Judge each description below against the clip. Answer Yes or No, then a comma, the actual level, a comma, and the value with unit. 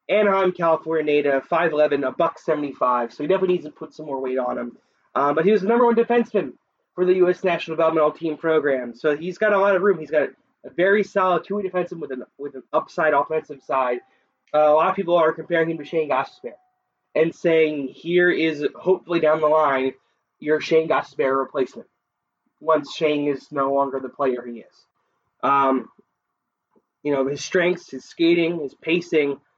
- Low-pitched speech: No, medium, 160 Hz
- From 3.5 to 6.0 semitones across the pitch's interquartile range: Yes, average, 4.0 semitones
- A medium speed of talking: Yes, average, 195 wpm